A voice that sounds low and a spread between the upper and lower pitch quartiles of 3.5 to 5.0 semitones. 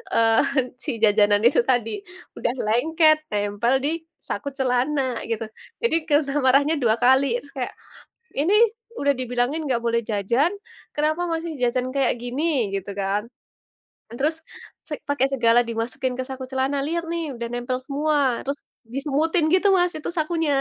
No: very high, 265 Hz; average, 4.3 semitones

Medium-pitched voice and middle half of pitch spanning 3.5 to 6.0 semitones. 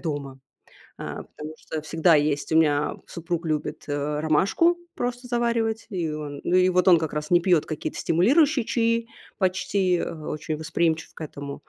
Yes: medium, 165 Hz; average, 4.6 semitones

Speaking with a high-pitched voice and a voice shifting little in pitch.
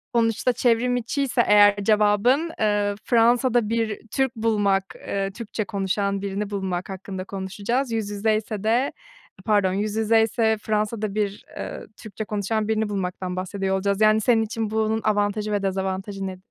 Yes: high, 210 Hz; narrow, 2.1 semitones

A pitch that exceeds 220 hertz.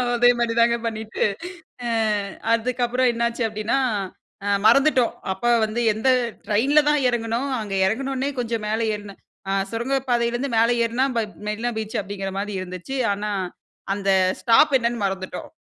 Yes: high, 230 Hz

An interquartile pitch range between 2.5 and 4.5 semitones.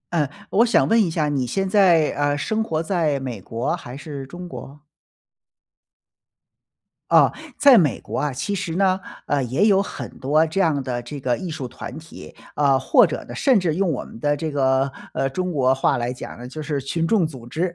No: average, 5.1 semitones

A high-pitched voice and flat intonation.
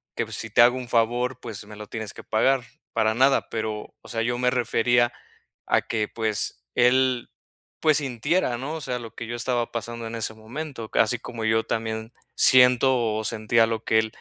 No: low, 115 Hz; narrow, 2.1 semitones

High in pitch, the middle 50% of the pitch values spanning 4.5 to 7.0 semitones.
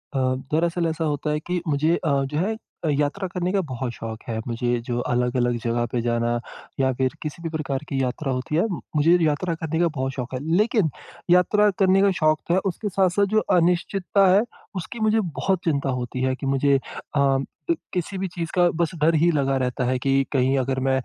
No: medium, 155 Hz; average, 5.1 semitones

